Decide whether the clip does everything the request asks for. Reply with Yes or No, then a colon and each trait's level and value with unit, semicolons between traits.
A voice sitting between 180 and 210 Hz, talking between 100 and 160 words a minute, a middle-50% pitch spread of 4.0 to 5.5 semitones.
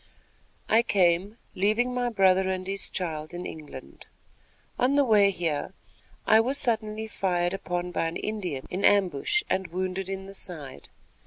No: high, 190 Hz; average, 155 wpm; average, 3.5 semitones